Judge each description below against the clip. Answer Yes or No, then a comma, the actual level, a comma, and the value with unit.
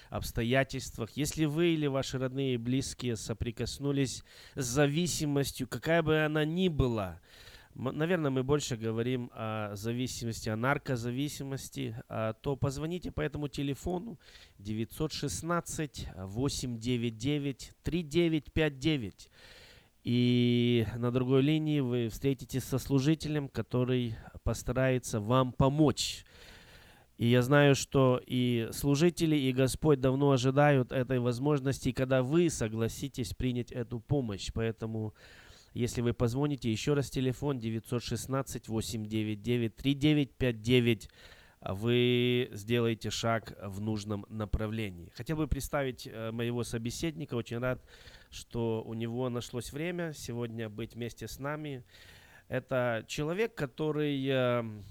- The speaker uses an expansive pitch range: No, average, 3.8 semitones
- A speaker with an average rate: No, slow, 105 wpm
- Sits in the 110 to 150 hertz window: Yes, low, 125 Hz